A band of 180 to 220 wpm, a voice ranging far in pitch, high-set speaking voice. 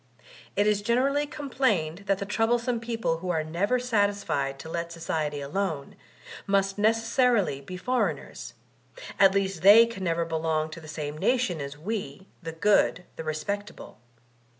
No: average, 150 wpm; wide, 5.9 semitones; high, 195 Hz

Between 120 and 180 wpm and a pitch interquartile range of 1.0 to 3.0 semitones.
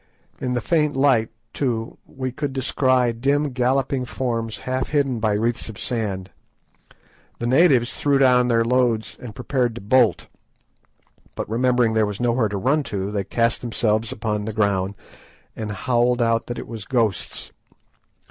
Yes: average, 160 wpm; average, 2.7 semitones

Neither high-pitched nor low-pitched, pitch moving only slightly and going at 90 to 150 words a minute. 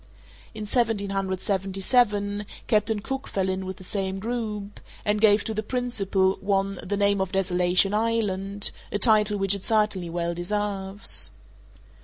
No: high, 200 Hz; narrow, 1.7 semitones; average, 140 wpm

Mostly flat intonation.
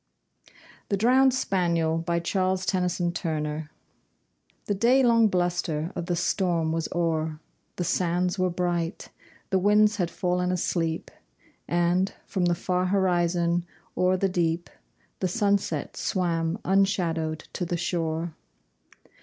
Yes: narrow, 2.1 semitones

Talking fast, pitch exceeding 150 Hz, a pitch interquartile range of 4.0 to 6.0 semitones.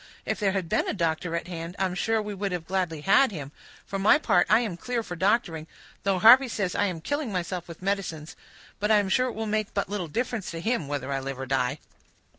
Yes: fast, 245 wpm; high, 190 Hz; average, 4.4 semitones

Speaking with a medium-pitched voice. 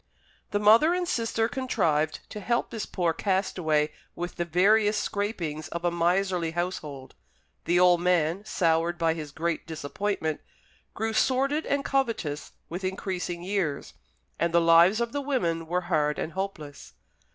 Yes: medium, 180 Hz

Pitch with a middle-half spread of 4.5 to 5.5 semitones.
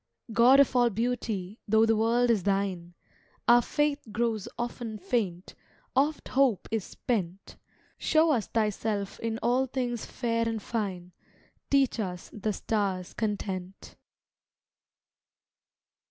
No: average, 3.4 semitones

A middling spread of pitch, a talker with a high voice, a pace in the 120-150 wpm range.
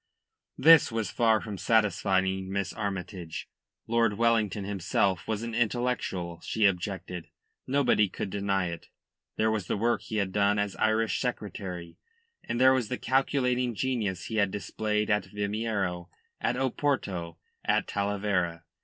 No: average, 3.4 semitones; low, 105 Hz; average, 140 wpm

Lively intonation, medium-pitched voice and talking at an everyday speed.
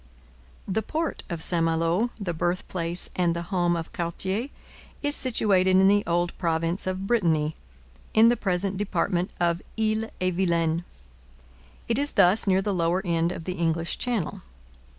No: average, 3.1 semitones; medium, 180 Hz; average, 155 wpm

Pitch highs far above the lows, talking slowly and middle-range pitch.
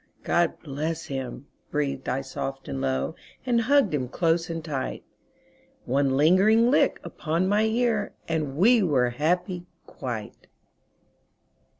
Yes: wide, 5.8 semitones; slow, 125 wpm; medium, 160 Hz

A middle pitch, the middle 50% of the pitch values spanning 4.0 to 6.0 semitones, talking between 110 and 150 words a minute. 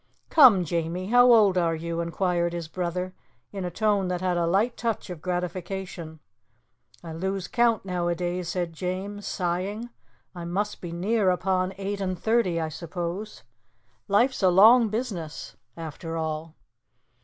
No: medium, 180 Hz; average, 2.9 semitones; average, 145 wpm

